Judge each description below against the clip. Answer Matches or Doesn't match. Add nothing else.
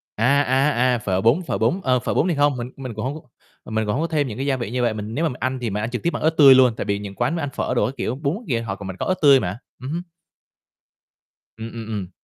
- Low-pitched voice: Matches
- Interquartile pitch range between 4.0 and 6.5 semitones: Matches